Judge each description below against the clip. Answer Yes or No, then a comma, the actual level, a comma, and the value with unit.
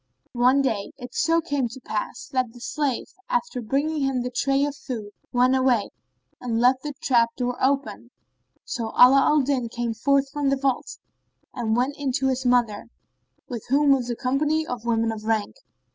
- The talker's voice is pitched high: Yes, very high, 255 Hz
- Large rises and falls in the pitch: No, narrow, 2.6 semitones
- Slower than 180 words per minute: No, average, 185 wpm